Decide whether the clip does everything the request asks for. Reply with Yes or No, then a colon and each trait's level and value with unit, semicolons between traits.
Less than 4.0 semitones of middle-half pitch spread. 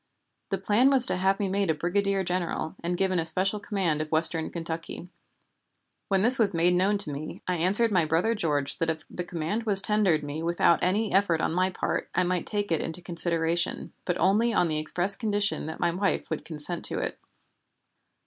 Yes: average, 3.4 semitones